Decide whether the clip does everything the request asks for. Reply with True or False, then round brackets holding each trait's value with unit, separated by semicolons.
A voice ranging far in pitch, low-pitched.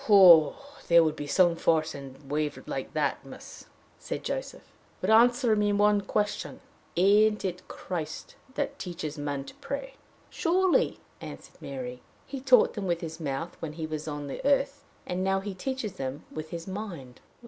False (6.0 semitones; 180 Hz)